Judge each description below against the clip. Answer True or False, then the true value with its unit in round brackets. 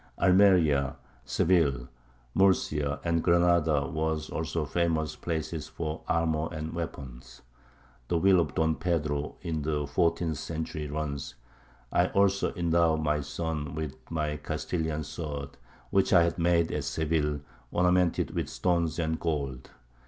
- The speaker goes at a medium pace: False (130 wpm)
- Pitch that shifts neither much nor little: False (2.2 semitones)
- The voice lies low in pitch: True (80 Hz)